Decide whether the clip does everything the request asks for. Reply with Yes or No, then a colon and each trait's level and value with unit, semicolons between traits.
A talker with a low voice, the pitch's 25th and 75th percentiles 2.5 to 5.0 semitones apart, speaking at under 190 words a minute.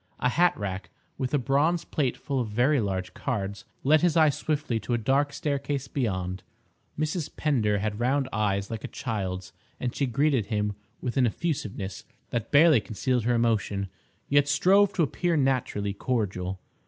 No: low, 125 Hz; wide, 5.6 semitones; average, 165 wpm